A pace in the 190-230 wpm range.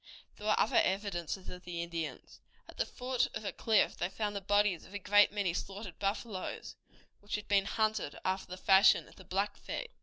Yes: average, 200 wpm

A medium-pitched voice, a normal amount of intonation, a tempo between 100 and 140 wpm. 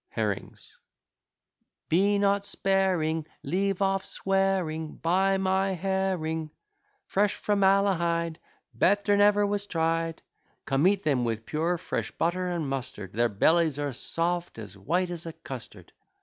Yes: medium, 175 Hz; average, 3.7 semitones; slow, 135 wpm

